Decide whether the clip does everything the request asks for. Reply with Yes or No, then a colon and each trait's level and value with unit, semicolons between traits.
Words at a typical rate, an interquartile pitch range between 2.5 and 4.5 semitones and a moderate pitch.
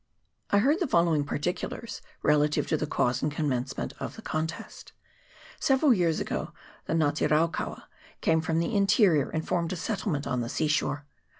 Yes: average, 180 wpm; average, 3.9 semitones; medium, 160 Hz